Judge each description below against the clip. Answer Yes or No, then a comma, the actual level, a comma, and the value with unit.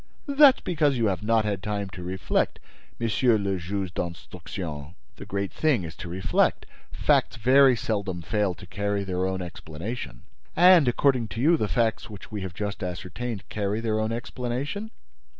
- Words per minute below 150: No, average, 170 wpm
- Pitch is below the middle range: Yes, low, 105 Hz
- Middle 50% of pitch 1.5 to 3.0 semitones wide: No, average, 4.6 semitones